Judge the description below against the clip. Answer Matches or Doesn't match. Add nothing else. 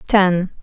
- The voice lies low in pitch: Doesn't match